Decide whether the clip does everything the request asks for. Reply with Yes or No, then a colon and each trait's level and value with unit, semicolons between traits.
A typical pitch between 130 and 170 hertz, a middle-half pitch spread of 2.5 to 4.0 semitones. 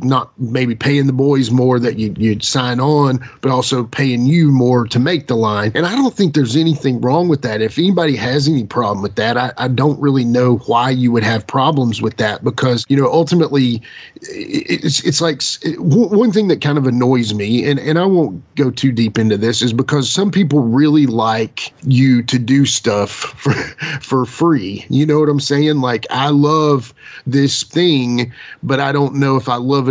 Yes: low, 135 Hz; average, 3.4 semitones